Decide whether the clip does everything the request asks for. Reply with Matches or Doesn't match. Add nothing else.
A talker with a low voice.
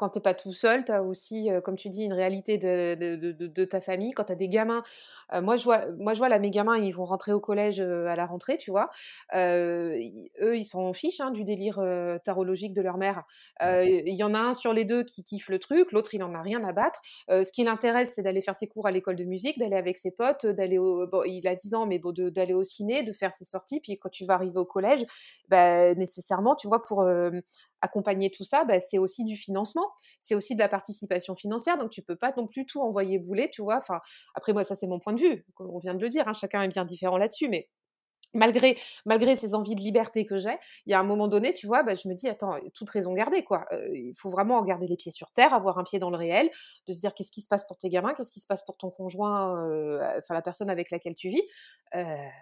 Doesn't match